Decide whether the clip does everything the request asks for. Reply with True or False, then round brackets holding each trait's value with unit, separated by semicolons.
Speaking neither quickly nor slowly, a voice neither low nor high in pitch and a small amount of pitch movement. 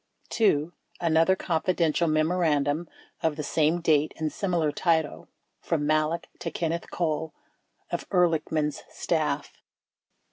False (120 wpm; 160 Hz; 1.8 semitones)